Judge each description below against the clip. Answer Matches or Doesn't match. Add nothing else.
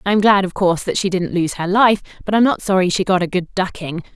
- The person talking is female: Matches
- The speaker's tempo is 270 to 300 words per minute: Matches